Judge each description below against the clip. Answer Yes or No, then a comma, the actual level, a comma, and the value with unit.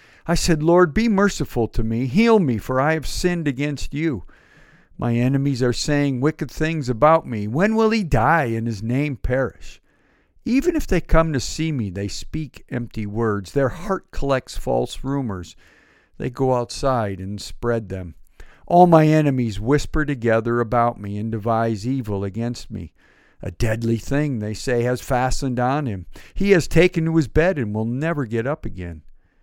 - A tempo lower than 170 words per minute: No, average, 175 wpm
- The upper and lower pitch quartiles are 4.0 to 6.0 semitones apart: Yes, wide, 5.6 semitones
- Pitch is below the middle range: Yes, low, 130 Hz